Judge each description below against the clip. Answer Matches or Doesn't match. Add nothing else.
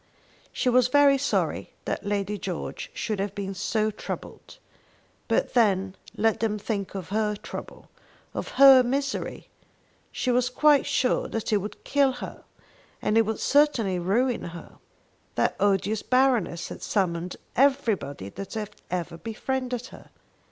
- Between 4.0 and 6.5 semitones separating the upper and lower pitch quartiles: Matches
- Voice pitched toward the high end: Matches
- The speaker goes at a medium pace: Matches